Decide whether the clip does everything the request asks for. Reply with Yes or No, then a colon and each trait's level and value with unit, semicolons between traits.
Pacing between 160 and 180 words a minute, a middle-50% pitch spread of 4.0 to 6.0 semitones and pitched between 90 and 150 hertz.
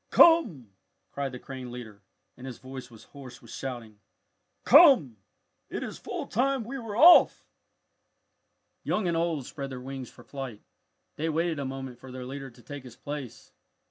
Yes: average, 170 wpm; average, 4.8 semitones; low, 135 Hz